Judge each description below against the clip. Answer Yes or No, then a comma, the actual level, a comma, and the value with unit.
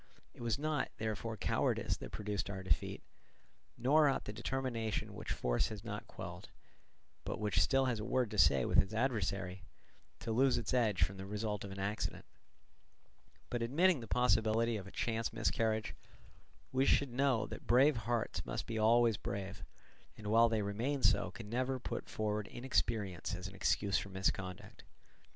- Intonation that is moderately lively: Yes, average, 3.4 semitones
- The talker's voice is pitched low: Yes, low, 110 Hz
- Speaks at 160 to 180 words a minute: Yes, average, 170 wpm